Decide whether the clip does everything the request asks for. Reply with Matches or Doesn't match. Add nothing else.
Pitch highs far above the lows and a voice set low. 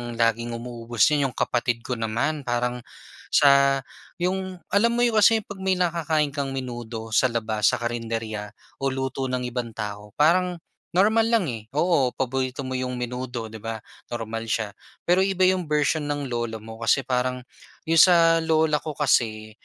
Matches